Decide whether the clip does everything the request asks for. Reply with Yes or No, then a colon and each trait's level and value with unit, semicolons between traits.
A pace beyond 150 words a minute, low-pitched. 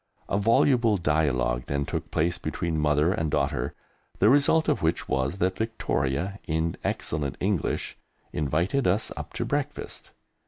No: average, 145 wpm; very low, 80 Hz